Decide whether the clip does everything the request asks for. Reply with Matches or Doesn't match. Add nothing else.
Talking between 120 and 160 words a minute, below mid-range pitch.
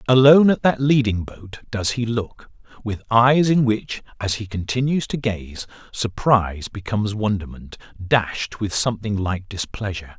Matches